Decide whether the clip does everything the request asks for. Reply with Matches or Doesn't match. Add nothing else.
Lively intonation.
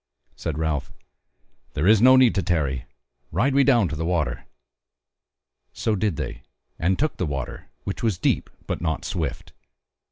Matches